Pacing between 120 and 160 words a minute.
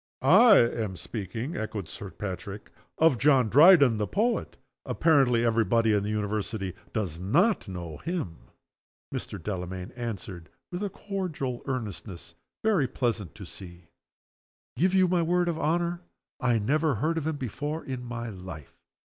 Yes: average, 150 wpm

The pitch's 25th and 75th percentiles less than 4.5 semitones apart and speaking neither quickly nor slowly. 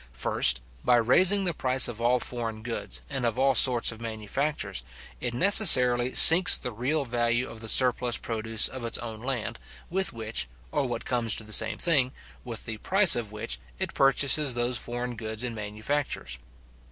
Yes: average, 3.1 semitones; average, 175 wpm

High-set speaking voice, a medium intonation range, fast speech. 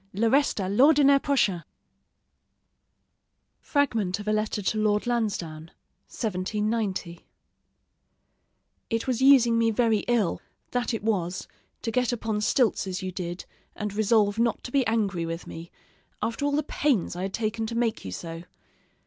No: high, 215 Hz; average, 4.1 semitones; average, 150 wpm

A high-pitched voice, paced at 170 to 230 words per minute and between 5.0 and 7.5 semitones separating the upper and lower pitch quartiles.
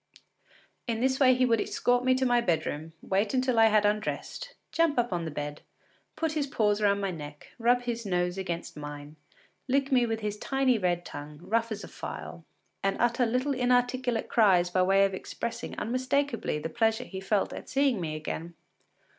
Yes: high, 225 Hz; average, 190 wpm; wide, 5.6 semitones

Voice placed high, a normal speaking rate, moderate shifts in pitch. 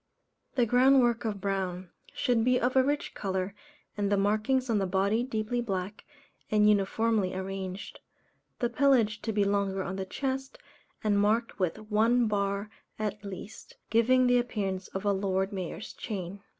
Yes: high, 210 Hz; average, 165 wpm; average, 3.5 semitones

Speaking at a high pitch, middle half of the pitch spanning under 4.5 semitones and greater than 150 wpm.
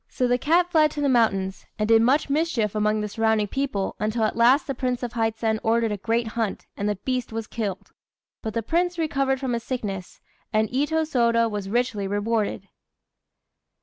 Yes: high, 230 Hz; average, 3.6 semitones; average, 190 wpm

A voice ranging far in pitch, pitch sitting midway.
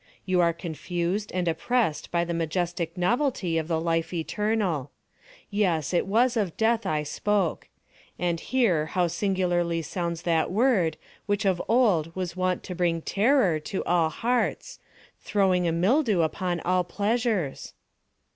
No: average, 3.7 semitones; medium, 180 Hz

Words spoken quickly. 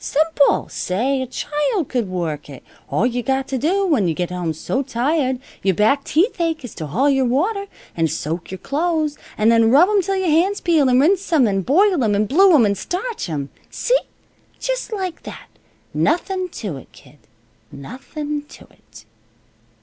No: average, 190 wpm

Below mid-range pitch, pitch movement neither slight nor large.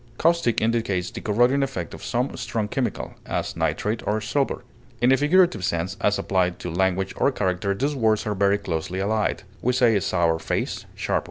Yes: low, 110 Hz; average, 4.8 semitones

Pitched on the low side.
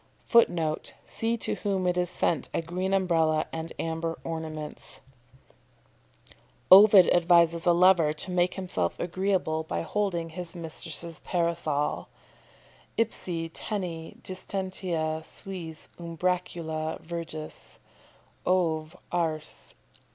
No: medium, 170 Hz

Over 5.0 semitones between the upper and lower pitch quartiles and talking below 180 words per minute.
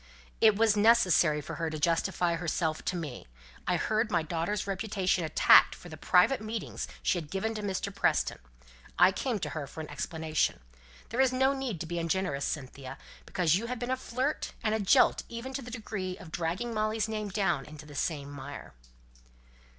No: wide, 5.6 semitones; average, 185 wpm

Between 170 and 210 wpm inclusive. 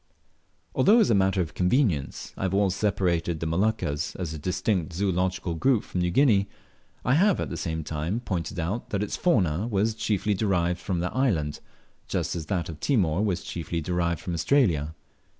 Yes: average, 185 wpm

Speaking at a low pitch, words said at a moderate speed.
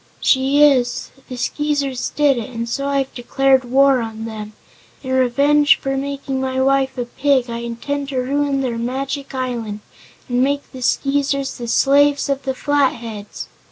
No: very high, 265 Hz; average, 165 wpm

